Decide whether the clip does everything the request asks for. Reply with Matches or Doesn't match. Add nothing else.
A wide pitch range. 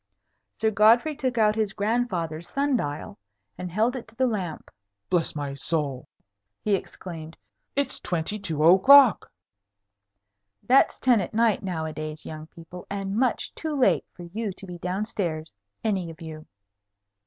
Matches